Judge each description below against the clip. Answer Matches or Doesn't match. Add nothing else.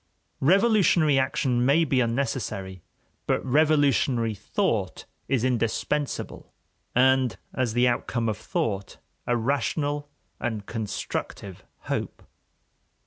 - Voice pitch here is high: Doesn't match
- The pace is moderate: Doesn't match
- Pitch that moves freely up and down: Doesn't match